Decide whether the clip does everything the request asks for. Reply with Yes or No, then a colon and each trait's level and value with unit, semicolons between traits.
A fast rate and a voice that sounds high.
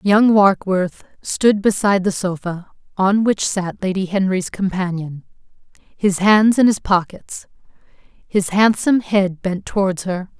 No: slow, 135 wpm; high, 195 Hz